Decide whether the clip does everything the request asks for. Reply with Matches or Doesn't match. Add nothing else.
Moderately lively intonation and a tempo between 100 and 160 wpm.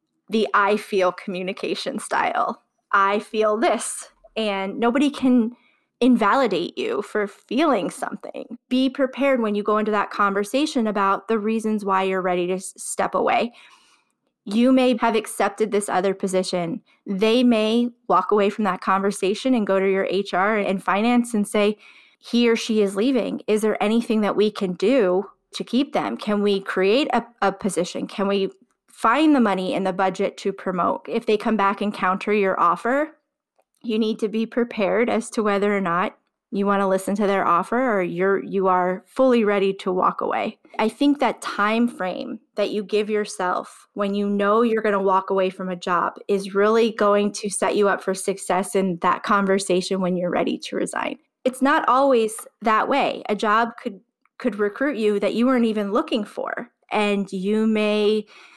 Doesn't match